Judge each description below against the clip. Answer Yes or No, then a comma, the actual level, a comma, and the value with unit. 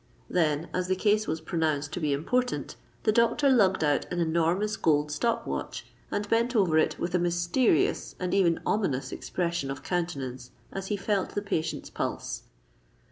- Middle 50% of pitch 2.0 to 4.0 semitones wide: No, average, 4.6 semitones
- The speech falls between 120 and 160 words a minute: No, average, 170 wpm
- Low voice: No, medium, 175 Hz